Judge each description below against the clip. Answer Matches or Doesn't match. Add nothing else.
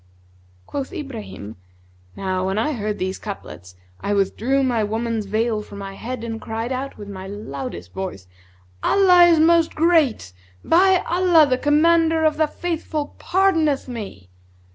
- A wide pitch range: Matches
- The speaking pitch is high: Matches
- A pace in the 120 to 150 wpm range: Matches